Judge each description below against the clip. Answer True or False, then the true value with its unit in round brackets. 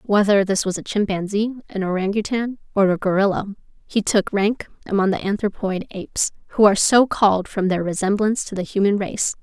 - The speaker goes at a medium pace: True (180 wpm)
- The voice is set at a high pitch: True (200 Hz)